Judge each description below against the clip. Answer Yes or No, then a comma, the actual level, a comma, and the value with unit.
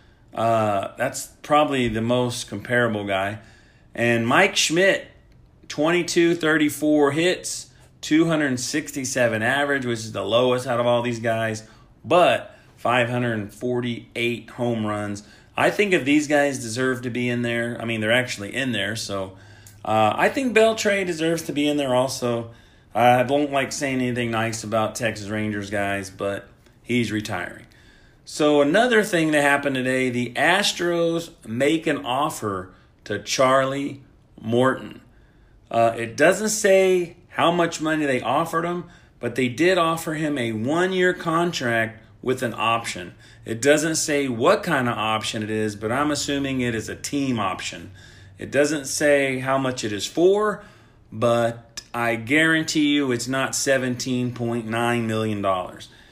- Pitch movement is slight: No, average, 4.6 semitones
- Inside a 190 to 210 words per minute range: No, average, 145 wpm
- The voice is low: Yes, low, 125 Hz